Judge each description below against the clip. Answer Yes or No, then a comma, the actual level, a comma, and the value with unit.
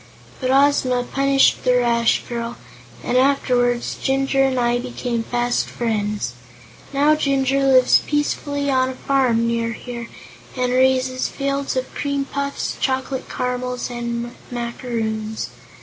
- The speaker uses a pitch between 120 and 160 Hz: No, very high, 255 Hz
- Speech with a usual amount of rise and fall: No, narrow, 2.2 semitones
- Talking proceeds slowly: Yes, slow, 125 wpm